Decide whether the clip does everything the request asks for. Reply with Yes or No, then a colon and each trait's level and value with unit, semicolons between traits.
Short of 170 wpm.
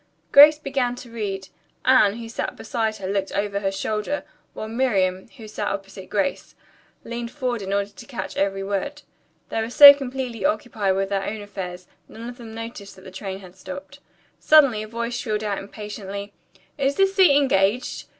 No: average, 180 wpm